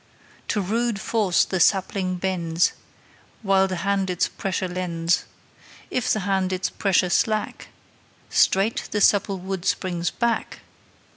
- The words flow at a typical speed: No, slow, 130 wpm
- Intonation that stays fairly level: Yes, narrow, 1.7 semitones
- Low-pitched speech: No, high, 190 Hz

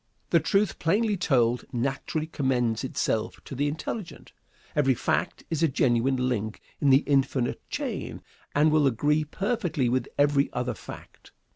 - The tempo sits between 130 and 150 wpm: Yes, average, 145 wpm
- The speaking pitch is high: No, medium, 140 Hz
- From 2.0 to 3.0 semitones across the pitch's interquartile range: No, average, 3.9 semitones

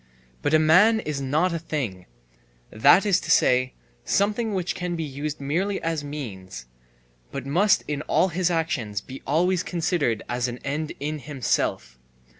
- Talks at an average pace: Yes, average, 160 wpm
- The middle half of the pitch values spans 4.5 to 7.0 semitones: Yes, average, 5.2 semitones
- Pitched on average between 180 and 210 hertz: No, medium, 150 Hz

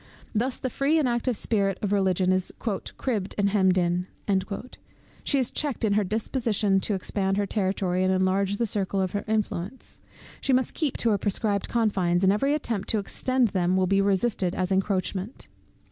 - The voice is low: No, high, 200 Hz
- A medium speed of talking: Yes, average, 185 wpm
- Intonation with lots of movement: No, average, 3.4 semitones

